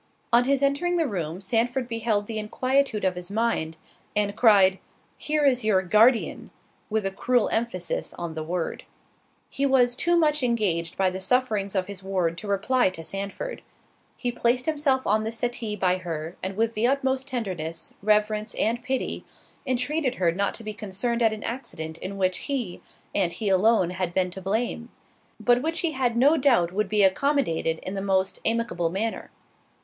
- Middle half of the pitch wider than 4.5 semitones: Yes, average, 4.9 semitones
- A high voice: Yes, high, 215 Hz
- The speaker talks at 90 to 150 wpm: No, average, 180 wpm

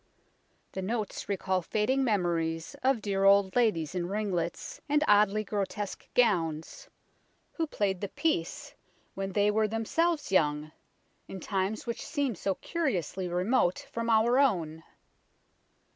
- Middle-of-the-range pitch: No, high, 200 Hz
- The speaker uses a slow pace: Yes, slow, 130 wpm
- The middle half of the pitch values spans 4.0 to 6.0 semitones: Yes, average, 4.4 semitones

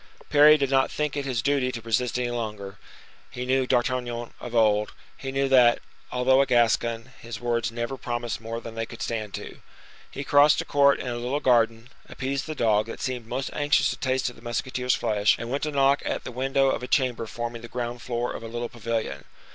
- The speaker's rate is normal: No, fast, 220 wpm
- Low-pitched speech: Yes, low, 120 Hz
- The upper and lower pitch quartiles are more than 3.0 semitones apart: No, narrow, 2.5 semitones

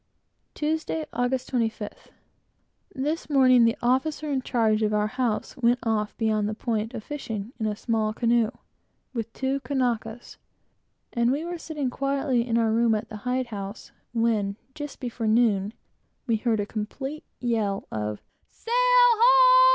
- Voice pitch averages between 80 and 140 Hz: No, high, 235 Hz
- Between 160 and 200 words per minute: No, average, 150 wpm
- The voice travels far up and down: No, average, 3.9 semitones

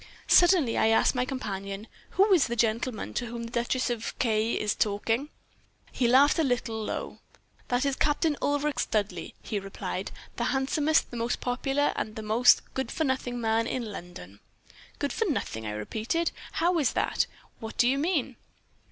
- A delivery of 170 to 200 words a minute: Yes, average, 180 wpm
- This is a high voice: Yes, high, 245 Hz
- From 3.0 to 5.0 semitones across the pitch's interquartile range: Yes, average, 4.2 semitones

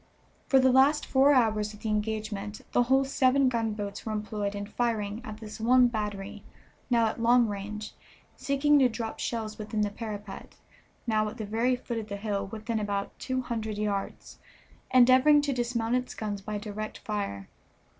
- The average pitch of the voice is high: Yes, high, 220 Hz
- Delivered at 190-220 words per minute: No, average, 175 wpm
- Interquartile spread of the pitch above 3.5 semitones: No, average, 2.9 semitones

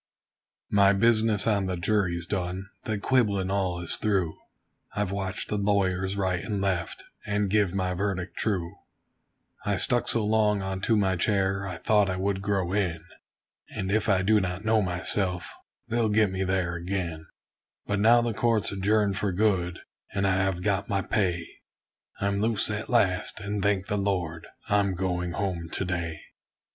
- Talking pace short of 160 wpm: No, average, 165 wpm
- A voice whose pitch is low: Yes, low, 100 Hz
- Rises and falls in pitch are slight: Yes, narrow, 2.2 semitones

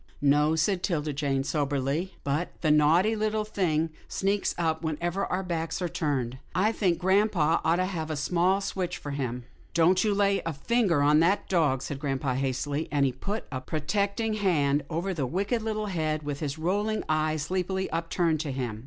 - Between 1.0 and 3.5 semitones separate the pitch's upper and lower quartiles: No, average, 4.6 semitones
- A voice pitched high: No, medium, 165 Hz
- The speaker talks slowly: No, average, 190 wpm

